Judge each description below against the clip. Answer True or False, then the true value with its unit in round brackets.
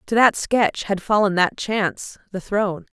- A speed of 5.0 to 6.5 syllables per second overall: False (4.6 syllables/s)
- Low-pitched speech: False (200 Hz)